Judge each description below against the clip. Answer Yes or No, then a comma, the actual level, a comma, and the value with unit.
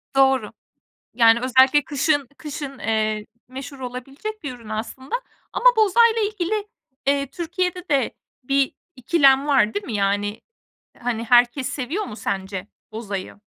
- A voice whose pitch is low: No, very high, 265 Hz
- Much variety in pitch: No, average, 4.7 semitones